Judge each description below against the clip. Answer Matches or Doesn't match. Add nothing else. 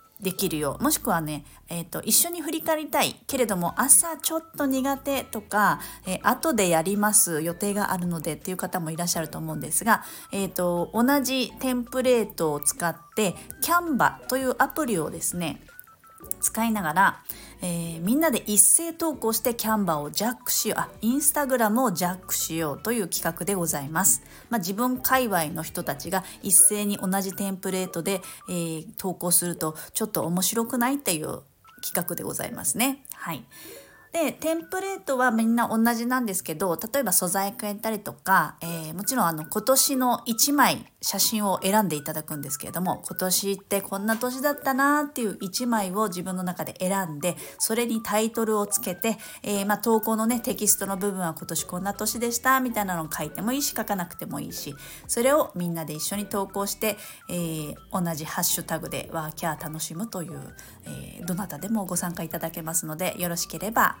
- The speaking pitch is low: Doesn't match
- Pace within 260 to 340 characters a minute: Doesn't match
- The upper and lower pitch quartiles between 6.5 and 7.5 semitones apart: Doesn't match